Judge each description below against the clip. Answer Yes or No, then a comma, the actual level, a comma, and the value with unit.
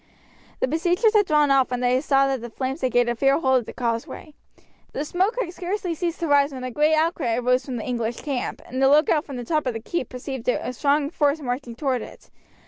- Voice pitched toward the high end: Yes, very high, 275 Hz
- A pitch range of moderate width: Yes, average, 3.7 semitones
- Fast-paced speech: Yes, fast, 240 wpm